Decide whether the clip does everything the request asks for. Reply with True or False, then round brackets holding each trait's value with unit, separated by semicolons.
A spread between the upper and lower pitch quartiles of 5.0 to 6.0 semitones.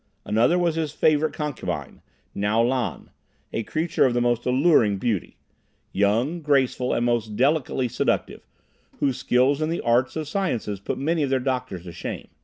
False (4.6 semitones)